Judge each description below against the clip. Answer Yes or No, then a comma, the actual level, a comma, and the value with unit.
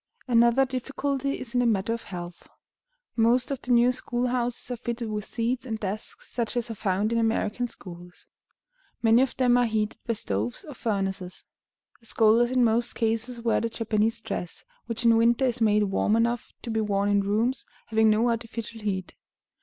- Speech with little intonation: Yes, narrow, 2.3 semitones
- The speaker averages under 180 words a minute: No, average, 185 wpm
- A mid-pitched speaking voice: No, high, 230 Hz